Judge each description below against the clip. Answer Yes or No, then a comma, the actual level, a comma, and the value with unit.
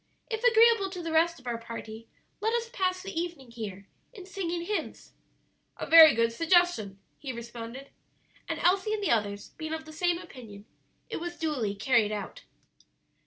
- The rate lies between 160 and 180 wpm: Yes, average, 170 wpm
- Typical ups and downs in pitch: No, wide, 8.1 semitones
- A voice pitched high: Yes, very high, 320 Hz